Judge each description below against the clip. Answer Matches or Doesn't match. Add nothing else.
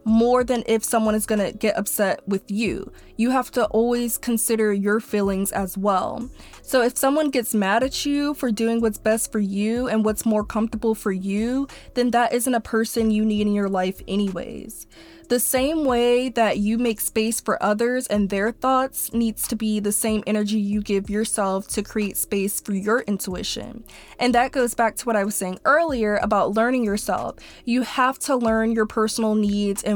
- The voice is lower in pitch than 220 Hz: Doesn't match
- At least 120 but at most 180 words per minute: Doesn't match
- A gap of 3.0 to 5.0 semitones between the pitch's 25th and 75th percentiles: Doesn't match